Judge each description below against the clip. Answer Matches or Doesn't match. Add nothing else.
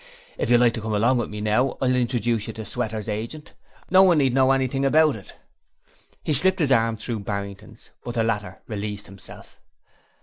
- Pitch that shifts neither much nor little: Matches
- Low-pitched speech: Matches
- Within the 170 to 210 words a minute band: Matches